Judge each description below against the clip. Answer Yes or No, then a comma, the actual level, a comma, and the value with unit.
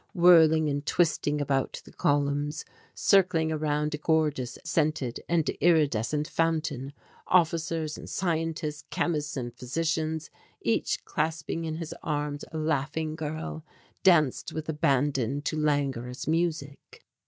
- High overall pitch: No, medium, 155 Hz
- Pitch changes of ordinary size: No, narrow, 2.0 semitones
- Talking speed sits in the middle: No, slow, 120 wpm